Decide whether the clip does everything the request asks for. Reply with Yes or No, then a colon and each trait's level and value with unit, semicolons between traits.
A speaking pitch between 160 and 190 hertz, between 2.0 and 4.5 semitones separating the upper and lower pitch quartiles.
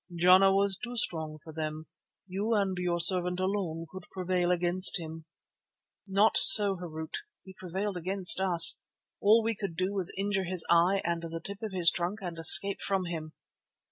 Yes: medium, 185 Hz; narrow, 2.6 semitones